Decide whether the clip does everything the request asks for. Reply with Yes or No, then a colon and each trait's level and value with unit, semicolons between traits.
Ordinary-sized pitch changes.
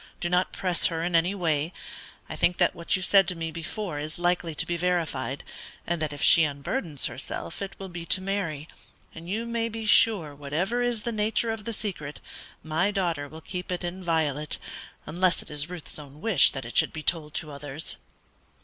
Yes: average, 3.9 semitones